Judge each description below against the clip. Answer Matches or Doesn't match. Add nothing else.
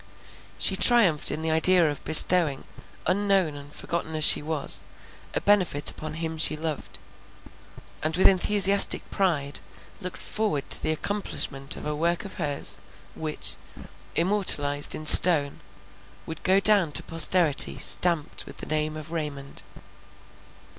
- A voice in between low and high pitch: Matches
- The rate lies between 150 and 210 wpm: Doesn't match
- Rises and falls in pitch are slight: Doesn't match